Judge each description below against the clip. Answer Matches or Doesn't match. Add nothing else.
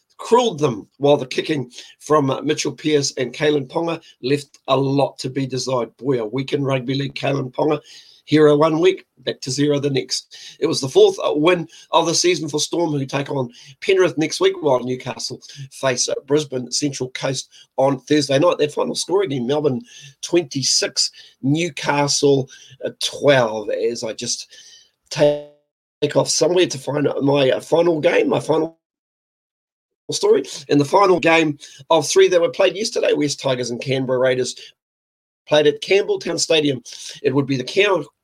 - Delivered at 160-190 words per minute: Matches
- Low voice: Doesn't match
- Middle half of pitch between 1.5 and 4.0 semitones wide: Matches